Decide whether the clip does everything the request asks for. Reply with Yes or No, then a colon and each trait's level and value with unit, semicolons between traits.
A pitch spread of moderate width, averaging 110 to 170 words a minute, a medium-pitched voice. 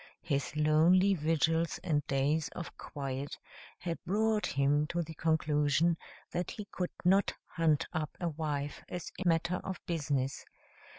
Yes: average, 3.0 semitones; average, 140 wpm; medium, 160 Hz